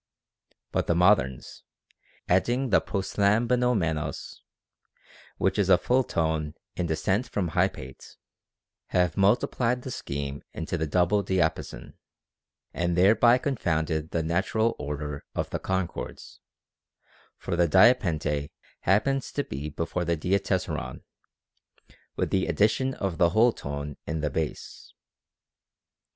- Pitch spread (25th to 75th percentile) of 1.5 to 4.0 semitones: No, average, 5.2 semitones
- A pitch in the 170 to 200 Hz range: No, very low, 90 Hz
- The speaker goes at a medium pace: No, slow, 120 wpm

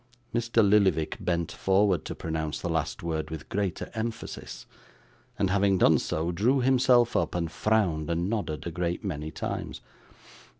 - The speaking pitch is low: Yes, very low, 95 Hz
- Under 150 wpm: No, average, 155 wpm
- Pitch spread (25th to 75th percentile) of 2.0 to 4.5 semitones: No, average, 5.0 semitones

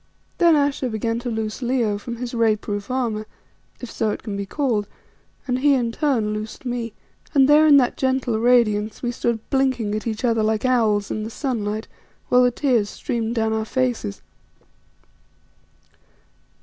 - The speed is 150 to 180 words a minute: Yes, average, 170 wpm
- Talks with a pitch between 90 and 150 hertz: No, high, 235 Hz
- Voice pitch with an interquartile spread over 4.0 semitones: No, average, 3.0 semitones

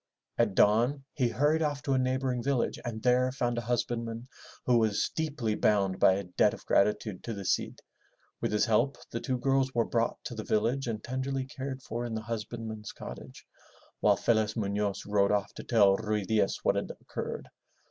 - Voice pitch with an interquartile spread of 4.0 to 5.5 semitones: No, average, 3.5 semitones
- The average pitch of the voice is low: Yes, low, 115 Hz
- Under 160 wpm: No, average, 195 wpm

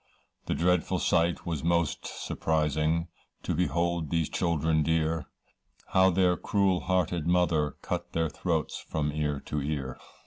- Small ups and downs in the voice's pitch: Yes, narrow, 2.3 semitones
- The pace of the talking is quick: No, slow, 135 wpm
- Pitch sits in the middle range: No, very low, 80 Hz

